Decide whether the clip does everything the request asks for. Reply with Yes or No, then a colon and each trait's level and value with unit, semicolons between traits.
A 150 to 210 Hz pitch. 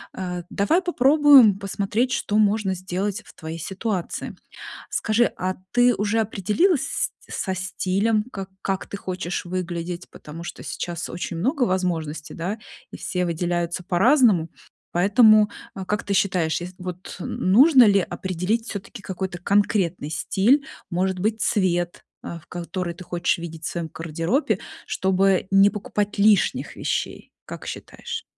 Yes: high, 190 Hz